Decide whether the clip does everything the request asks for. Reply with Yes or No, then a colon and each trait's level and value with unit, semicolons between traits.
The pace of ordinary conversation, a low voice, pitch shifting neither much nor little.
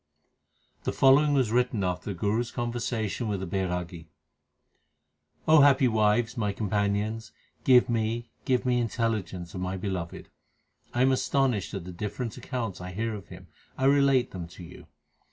Yes: average, 165 wpm; low, 110 Hz; average, 4.6 semitones